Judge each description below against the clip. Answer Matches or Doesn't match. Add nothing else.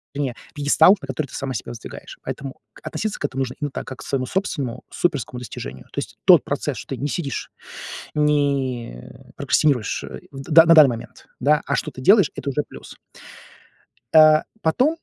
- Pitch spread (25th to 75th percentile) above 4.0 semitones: Doesn't match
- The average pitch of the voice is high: Doesn't match